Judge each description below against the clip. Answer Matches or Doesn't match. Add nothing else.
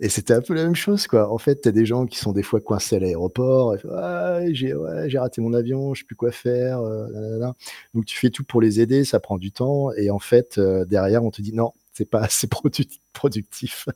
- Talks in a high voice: Doesn't match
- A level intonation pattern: Doesn't match